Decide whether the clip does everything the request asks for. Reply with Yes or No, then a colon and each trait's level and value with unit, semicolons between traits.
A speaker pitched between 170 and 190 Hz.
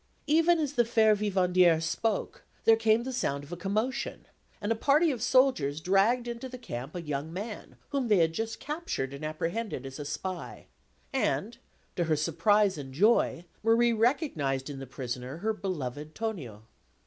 No: high, 200 Hz